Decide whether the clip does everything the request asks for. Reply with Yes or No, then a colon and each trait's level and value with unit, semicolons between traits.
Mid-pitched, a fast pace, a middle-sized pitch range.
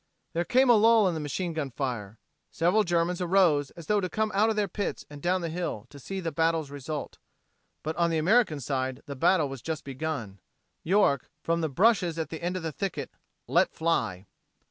Yes: medium, 165 Hz; fast, 210 wpm; average, 4.5 semitones